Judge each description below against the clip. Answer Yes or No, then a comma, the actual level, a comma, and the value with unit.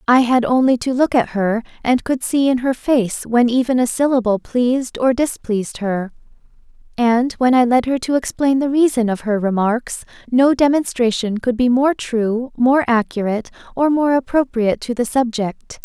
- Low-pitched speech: No, high, 245 Hz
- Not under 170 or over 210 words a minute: Yes, average, 180 wpm